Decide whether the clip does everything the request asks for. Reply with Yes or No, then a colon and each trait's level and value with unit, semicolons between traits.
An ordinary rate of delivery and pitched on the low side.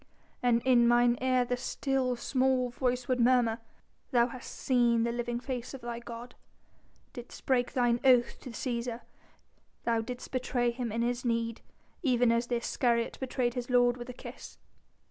No: average, 165 wpm; high, 245 Hz